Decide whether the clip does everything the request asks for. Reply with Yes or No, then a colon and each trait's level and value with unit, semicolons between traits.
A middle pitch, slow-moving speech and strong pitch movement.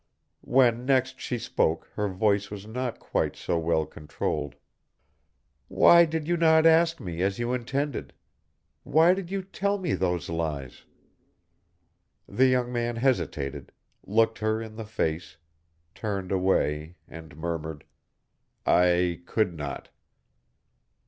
No: low, 110 Hz; slow, 125 wpm; wide, 7.6 semitones